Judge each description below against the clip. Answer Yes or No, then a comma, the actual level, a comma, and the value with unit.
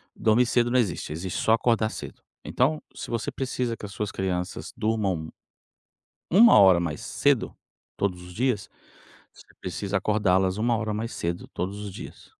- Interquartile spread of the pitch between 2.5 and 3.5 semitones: No, average, 3.9 semitones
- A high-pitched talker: No, low, 105 Hz